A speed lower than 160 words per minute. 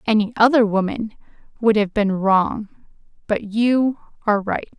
Yes: average, 140 wpm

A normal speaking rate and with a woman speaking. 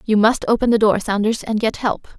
No: fast, 245 wpm; female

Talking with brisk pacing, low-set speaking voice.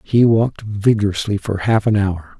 No: average, 175 wpm; low, 100 Hz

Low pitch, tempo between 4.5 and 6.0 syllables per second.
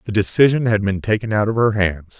Yes: low, 105 Hz; 5.9 syllables/s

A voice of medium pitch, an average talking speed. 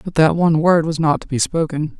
No: medium, 155 Hz; fast, 270 wpm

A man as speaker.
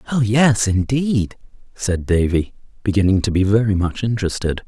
Yes: male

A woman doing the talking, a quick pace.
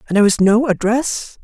No: male; fast, 210 wpm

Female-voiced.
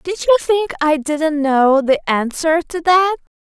Yes: female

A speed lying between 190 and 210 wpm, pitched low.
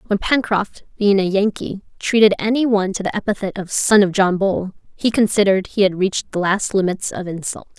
No: average, 200 wpm; high, 200 Hz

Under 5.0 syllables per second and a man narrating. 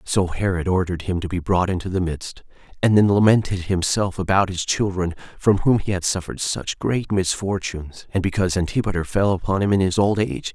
No: 5.7 syllables/s; male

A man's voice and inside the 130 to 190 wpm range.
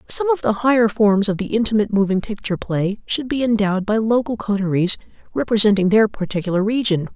No: female; average, 175 wpm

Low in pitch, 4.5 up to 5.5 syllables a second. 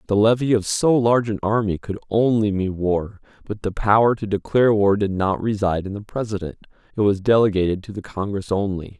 No: low, 105 Hz; 5.7 syllables/s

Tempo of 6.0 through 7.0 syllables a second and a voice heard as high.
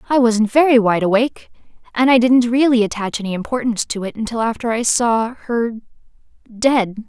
No: 5.5 syllables/s; high, 230 Hz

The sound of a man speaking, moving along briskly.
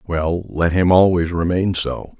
No: male; average, 165 wpm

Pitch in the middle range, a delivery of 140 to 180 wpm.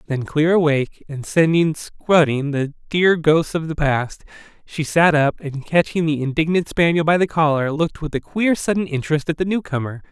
No: medium, 155 Hz; average, 190 wpm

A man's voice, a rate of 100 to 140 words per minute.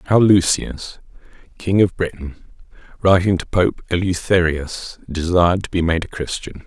Yes: male; slow, 135 wpm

